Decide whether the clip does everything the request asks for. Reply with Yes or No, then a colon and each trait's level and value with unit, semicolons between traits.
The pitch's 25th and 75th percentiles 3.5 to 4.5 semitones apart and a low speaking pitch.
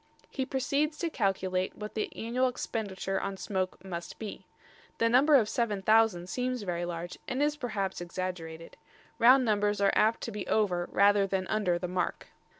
No: average, 4.2 semitones; high, 205 Hz